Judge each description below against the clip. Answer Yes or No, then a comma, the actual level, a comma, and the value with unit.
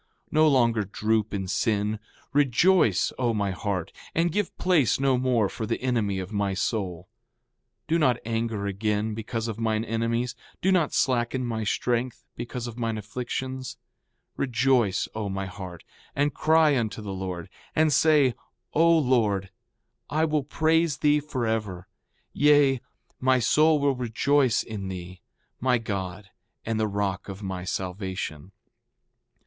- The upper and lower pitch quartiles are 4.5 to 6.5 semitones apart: Yes, average, 4.9 semitones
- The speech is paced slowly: No, average, 145 wpm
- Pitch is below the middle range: Yes, low, 115 Hz